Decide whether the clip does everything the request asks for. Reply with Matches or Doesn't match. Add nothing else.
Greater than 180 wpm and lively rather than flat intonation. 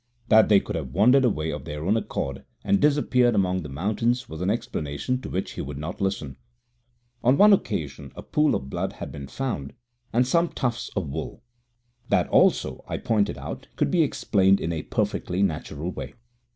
Matches